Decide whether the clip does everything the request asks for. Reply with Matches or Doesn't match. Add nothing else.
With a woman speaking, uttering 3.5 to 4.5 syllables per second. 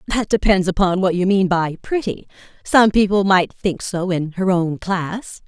Matches